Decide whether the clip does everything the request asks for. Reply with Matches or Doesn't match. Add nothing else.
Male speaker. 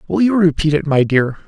Matches